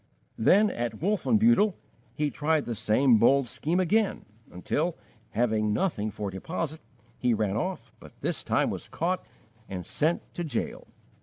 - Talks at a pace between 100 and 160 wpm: Yes, average, 145 wpm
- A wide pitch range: Yes, wide, 8.6 semitones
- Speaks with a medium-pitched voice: Yes, medium, 145 Hz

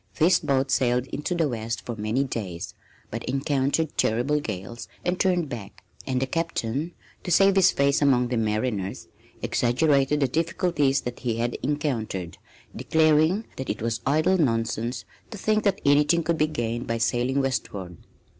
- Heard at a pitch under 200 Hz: Yes, low, 135 Hz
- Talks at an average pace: Yes, average, 160 wpm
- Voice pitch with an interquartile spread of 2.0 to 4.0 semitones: No, average, 5.2 semitones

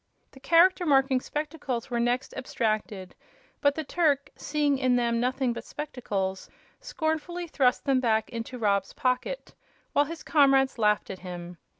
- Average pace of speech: Yes, average, 150 wpm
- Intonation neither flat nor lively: Yes, average, 4.3 semitones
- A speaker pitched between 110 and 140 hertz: No, very high, 260 Hz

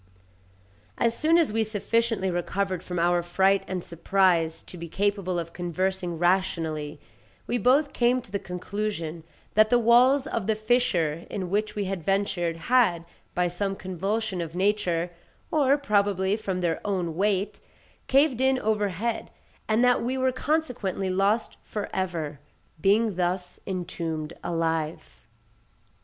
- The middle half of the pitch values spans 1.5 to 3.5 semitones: No, average, 4.1 semitones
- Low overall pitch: No, high, 195 Hz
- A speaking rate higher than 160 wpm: No, average, 140 wpm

